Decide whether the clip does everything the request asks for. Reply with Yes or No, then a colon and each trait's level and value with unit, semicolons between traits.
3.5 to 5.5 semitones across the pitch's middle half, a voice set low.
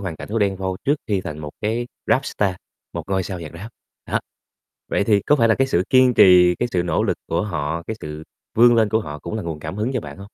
Yes: average, 4.7 semitones; low, 100 Hz